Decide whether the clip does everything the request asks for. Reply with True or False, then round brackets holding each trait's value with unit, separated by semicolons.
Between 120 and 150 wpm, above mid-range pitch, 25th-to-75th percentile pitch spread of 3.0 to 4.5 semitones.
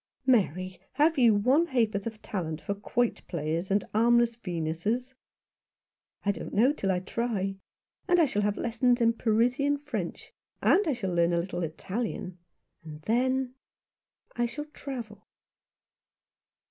False (145 wpm; 220 Hz; 5.0 semitones)